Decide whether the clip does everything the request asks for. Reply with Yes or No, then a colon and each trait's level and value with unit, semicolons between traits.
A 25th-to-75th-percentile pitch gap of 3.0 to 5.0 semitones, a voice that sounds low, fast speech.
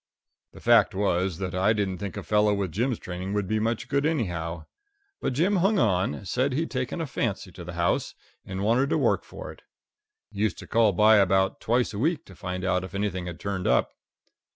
Yes: average, 4.5 semitones; low, 100 Hz; fast, 210 wpm